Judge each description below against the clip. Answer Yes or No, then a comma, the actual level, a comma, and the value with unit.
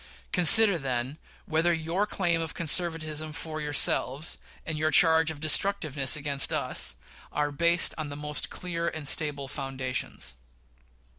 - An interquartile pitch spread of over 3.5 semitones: No, narrow, 2.5 semitones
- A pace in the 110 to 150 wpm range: Yes, slow, 135 wpm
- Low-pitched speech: No, medium, 155 Hz